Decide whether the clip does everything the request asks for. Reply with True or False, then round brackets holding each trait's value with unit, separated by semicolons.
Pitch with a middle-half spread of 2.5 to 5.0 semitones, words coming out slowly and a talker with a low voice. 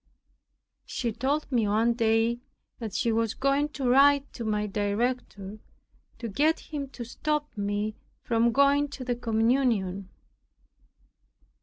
False (4.1 semitones; 130 wpm; 235 Hz)